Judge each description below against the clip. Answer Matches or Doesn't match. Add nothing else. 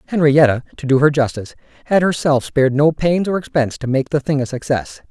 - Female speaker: Doesn't match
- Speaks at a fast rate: Matches